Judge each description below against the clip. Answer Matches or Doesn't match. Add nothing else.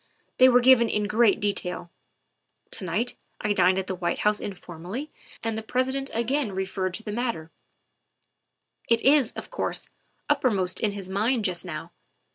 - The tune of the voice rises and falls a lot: Doesn't match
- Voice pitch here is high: Matches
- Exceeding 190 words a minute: Doesn't match